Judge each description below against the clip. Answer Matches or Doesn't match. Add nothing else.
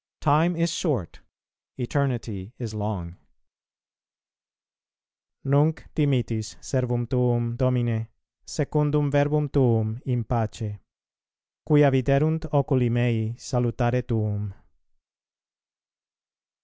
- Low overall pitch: Matches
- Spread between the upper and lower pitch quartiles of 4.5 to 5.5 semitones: Doesn't match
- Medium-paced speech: Doesn't match